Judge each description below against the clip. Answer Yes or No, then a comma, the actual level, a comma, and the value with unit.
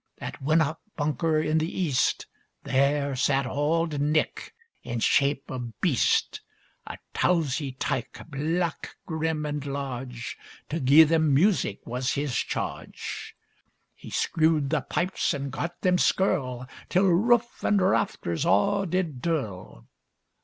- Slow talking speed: Yes, slow, 125 wpm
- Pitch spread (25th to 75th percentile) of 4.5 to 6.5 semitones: No, average, 3.8 semitones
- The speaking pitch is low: No, medium, 150 Hz